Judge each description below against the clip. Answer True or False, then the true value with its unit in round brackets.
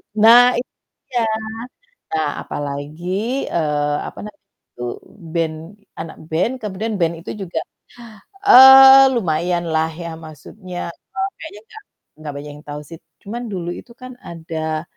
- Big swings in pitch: True (6.4 semitones)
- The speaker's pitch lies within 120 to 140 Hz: False (175 Hz)